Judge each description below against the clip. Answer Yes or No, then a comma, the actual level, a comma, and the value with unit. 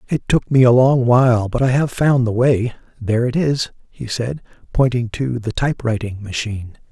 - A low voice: Yes, low, 120 Hz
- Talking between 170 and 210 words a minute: Yes, average, 190 wpm